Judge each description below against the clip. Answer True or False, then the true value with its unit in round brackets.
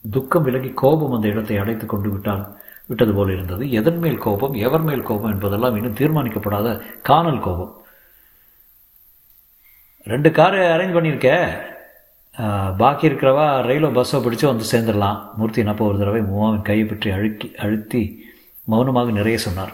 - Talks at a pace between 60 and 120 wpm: False (130 wpm)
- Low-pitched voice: True (115 Hz)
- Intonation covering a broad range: False (4.0 semitones)